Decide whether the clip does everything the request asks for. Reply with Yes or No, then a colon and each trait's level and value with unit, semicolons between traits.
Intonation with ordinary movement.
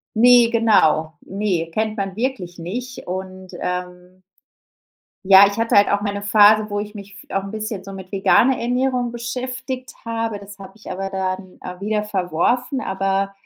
Yes: average, 3.3 semitones